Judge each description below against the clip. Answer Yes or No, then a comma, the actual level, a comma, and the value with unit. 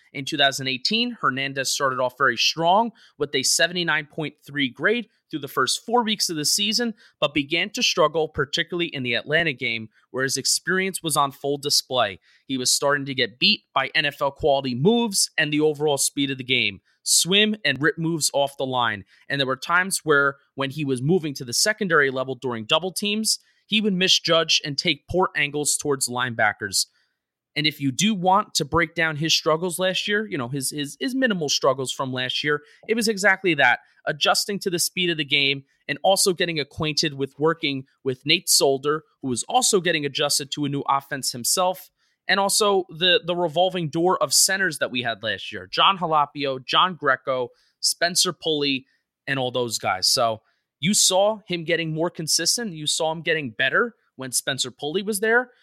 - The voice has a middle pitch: Yes, medium, 155 Hz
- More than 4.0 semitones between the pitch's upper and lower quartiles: Yes, average, 5.1 semitones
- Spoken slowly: No, average, 190 wpm